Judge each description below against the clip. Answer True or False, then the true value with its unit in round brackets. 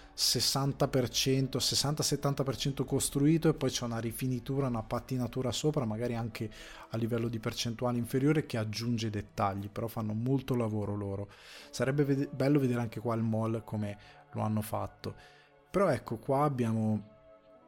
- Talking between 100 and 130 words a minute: False (145 wpm)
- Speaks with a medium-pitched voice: False (120 Hz)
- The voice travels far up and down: False (3.6 semitones)